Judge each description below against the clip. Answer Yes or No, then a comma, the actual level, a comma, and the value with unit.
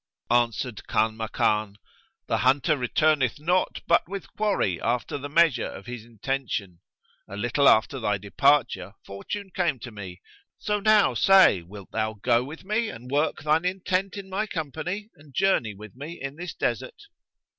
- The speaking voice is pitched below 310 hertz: Yes, low, 135 Hz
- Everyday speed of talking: Yes, average, 155 wpm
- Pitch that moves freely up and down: Yes, wide, 8.3 semitones